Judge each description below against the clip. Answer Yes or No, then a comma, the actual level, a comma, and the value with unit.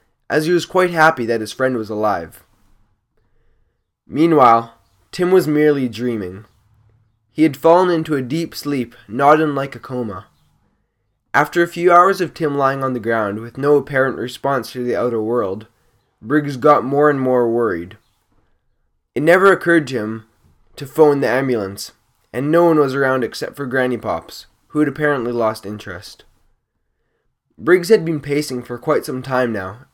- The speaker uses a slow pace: No, average, 165 wpm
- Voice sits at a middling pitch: No, low, 130 Hz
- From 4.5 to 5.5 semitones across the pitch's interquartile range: Yes, average, 5.1 semitones